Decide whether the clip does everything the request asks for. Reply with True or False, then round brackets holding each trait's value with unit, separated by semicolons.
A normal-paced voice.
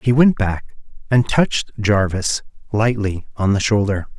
True (145 wpm)